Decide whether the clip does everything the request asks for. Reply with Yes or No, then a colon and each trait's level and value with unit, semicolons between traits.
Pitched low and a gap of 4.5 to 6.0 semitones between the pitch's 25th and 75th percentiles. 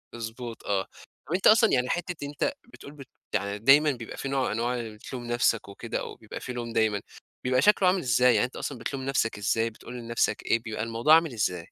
No: low, 120 Hz; average, 3.4 semitones